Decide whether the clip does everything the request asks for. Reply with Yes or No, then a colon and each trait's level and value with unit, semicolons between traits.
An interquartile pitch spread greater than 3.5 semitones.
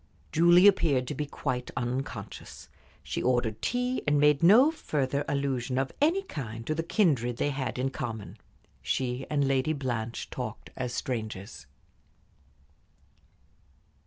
Yes: average, 4.0 semitones